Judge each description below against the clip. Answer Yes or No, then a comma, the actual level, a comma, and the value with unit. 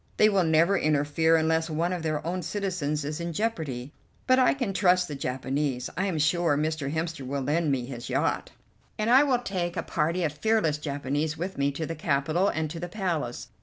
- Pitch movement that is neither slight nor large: Yes, average, 3.7 semitones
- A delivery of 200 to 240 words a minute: Yes, fast, 205 wpm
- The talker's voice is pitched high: No, medium, 160 Hz